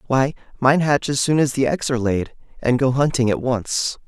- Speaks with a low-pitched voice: Yes, low, 130 Hz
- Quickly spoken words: Yes, fast, 220 wpm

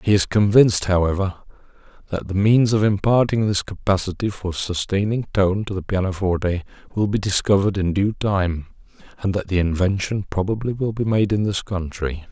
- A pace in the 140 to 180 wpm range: Yes, average, 165 wpm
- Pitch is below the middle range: Yes, low, 100 Hz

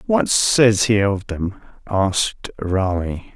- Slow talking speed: Yes, slow, 125 wpm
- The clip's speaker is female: No, male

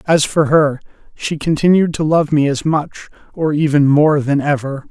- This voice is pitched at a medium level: Yes, medium, 150 Hz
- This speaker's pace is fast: No, average, 185 wpm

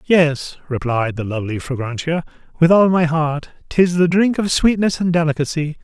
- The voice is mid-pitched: Yes, medium, 160 Hz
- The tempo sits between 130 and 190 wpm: Yes, average, 165 wpm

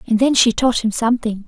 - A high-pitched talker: Yes, high, 230 Hz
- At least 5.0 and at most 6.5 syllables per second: Yes, 5.9 syllables/s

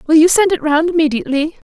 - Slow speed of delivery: No, fast, 210 wpm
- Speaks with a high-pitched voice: Yes, very high, 315 Hz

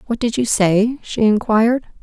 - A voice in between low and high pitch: No, high, 225 Hz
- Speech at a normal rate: Yes, average, 180 wpm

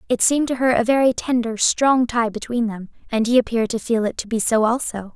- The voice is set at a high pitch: Yes, high, 235 Hz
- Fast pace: Yes, fast, 245 wpm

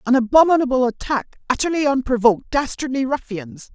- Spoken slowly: Yes, slow, 110 wpm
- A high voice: Yes, very high, 255 Hz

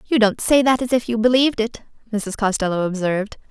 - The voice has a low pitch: No, high, 225 Hz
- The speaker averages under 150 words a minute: No, fast, 205 wpm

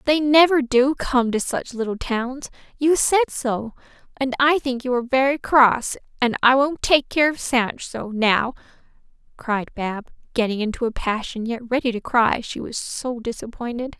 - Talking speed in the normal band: Yes, average, 175 wpm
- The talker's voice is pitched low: No, very high, 250 Hz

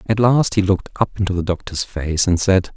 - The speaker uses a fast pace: Yes, fast, 240 wpm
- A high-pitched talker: No, very low, 95 Hz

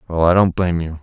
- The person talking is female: No, male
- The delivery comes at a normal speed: No, fast, 295 wpm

